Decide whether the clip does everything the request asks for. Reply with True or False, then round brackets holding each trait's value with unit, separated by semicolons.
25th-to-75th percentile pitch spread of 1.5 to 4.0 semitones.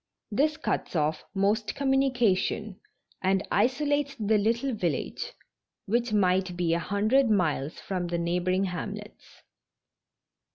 False (5.1 semitones)